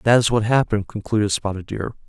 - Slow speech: No, average, 200 wpm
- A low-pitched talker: Yes, low, 110 Hz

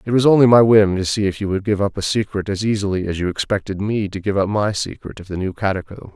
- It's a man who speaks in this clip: Yes, male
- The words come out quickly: Yes, fast, 285 wpm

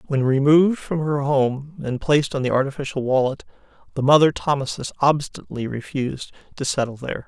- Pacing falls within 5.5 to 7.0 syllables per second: Yes, 6.0 syllables/s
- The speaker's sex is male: Yes, male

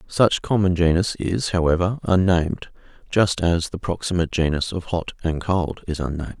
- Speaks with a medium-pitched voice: No, very low, 85 Hz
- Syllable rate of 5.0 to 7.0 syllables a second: Yes, 5.1 syllables/s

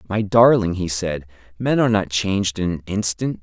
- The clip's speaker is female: No, male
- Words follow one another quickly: No, average, 195 wpm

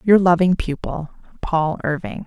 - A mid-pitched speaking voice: Yes, medium, 170 Hz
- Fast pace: No, slow, 135 wpm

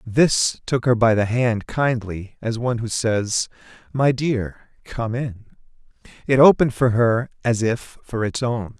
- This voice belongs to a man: Yes, male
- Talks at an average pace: Yes, average, 165 wpm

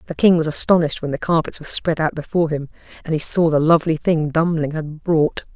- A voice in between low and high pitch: Yes, medium, 160 Hz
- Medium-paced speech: No, fast, 225 wpm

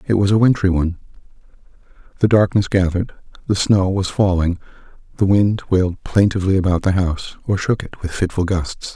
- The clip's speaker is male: Yes, male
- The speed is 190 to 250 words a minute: No, average, 165 wpm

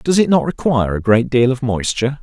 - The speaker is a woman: No, male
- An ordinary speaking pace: No, fast, 240 wpm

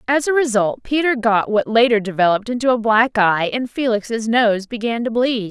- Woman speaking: Yes, female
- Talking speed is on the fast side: No, average, 195 wpm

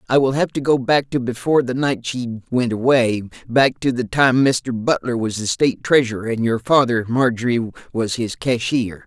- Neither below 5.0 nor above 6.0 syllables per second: Yes, 5.5 syllables/s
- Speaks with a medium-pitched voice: No, low, 120 Hz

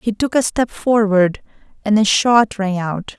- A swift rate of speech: No, average, 190 wpm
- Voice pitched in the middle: No, high, 210 Hz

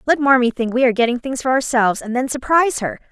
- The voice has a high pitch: Yes, very high, 255 Hz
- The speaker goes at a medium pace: No, fast, 250 wpm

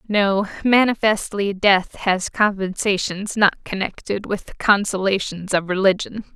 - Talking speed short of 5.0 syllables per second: Yes, 4.3 syllables/s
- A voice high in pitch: Yes, high, 200 Hz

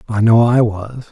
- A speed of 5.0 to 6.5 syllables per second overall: No, 4.6 syllables/s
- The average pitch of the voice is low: Yes, low, 115 Hz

